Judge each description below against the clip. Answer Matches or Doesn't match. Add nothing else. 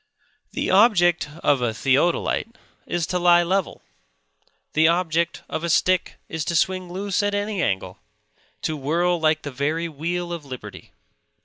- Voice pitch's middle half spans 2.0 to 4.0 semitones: Matches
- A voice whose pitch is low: Doesn't match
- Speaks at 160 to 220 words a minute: Doesn't match